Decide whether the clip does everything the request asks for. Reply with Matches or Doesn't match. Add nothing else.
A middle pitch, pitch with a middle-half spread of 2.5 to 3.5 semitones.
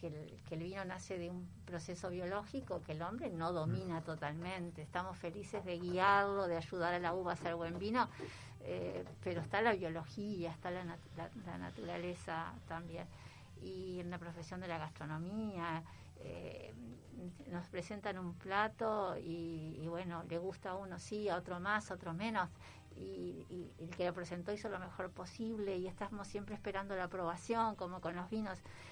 Matches